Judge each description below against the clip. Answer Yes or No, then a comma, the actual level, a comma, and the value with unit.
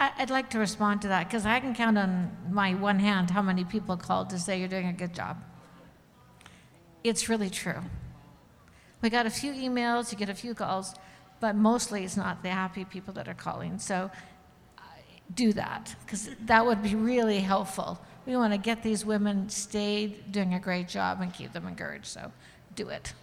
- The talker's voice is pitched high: Yes, high, 205 Hz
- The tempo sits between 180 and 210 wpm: Yes, average, 195 wpm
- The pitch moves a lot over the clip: No, average, 3.2 semitones